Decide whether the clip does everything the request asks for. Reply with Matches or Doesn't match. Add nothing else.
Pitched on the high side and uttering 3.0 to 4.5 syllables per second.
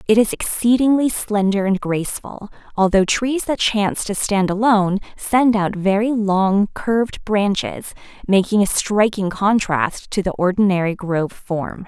Matches